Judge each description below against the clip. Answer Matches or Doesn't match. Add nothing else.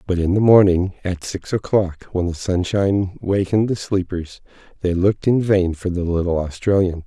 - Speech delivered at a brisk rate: Doesn't match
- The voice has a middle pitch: Doesn't match